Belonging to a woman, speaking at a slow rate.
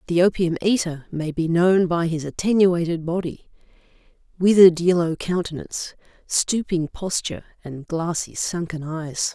Yes: female; slow, 120 wpm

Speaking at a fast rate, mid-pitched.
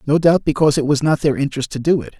Yes: fast, 300 wpm; medium, 145 Hz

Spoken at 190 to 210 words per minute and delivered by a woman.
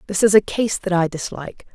No: fast, 240 wpm; female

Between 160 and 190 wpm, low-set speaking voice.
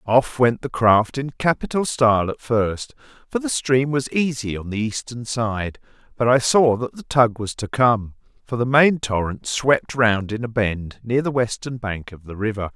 No: average, 200 wpm; low, 120 Hz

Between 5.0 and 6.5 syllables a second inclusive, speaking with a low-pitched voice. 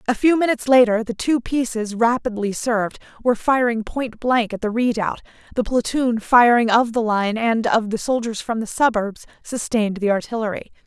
No: 5.2 syllables/s; high, 230 Hz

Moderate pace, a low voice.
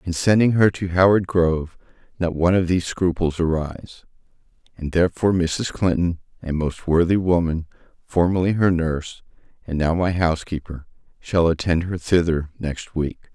Yes: average, 150 wpm; very low, 85 Hz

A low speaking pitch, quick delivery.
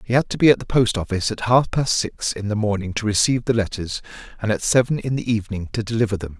Yes: low, 110 Hz; fast, 265 wpm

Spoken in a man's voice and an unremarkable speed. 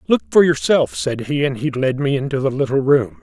No: male; fast, 240 wpm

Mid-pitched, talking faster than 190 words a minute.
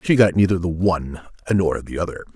No: very low, 90 Hz; fast, 205 wpm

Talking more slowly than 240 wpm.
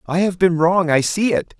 No: fast, 265 wpm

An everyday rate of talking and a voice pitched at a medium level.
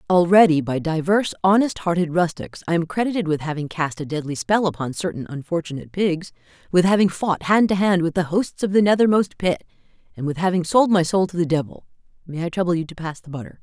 No: fast, 210 wpm; medium, 175 Hz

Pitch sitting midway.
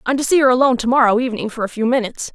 No: high, 245 Hz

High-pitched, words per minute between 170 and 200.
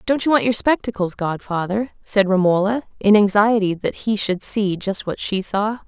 Yes: high, 205 Hz; average, 185 wpm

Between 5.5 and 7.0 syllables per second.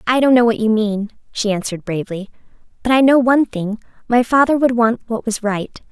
Yes: 5.7 syllables/s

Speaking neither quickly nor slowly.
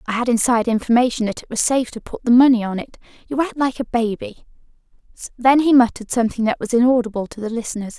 No: fast, 220 wpm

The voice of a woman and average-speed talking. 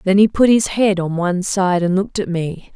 No: female; fast, 260 wpm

